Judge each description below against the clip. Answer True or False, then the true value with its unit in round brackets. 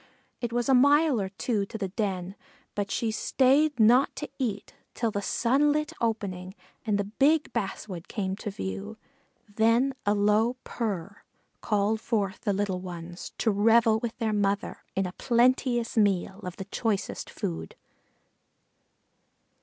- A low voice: False (215 Hz)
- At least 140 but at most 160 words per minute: True (150 wpm)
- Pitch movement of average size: True (3.5 semitones)